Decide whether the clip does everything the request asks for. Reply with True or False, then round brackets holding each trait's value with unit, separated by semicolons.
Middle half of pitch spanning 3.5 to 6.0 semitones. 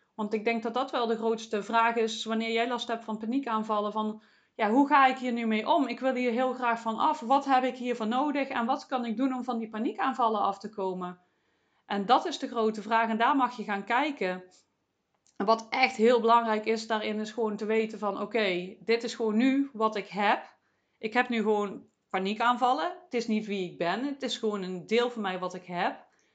False (2.6 semitones)